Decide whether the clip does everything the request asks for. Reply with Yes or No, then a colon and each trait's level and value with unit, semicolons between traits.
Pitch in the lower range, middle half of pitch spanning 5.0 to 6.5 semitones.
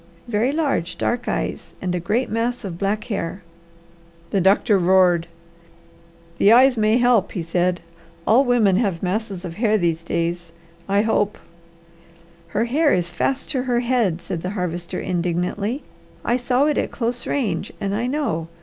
No: high, 200 Hz; wide, 5.5 semitones